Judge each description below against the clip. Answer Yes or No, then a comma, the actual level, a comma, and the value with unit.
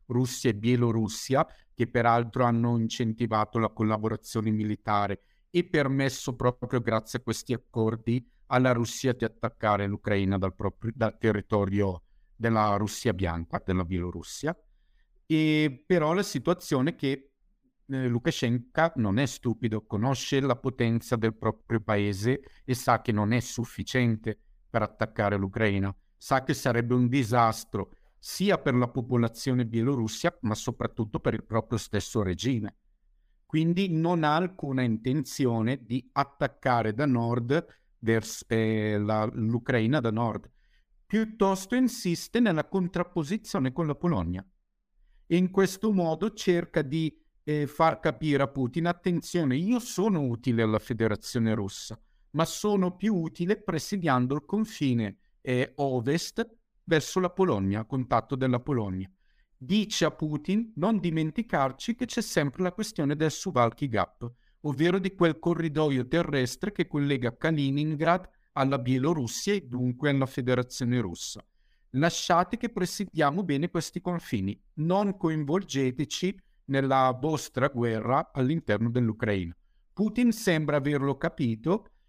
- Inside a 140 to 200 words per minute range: No, average, 125 wpm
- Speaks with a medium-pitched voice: No, low, 130 Hz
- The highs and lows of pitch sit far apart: Yes, wide, 6.3 semitones